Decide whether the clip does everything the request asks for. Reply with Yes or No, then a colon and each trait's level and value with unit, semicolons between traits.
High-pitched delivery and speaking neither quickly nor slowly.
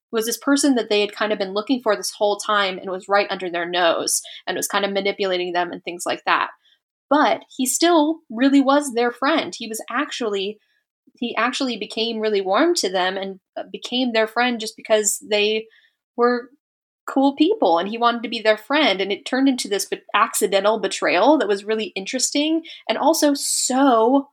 Yes: high, 230 Hz; average, 190 wpm